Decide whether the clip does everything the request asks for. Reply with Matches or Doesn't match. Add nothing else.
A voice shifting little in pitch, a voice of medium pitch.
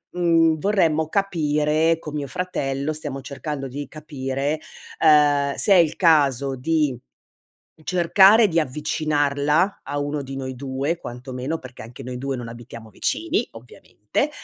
Doesn't match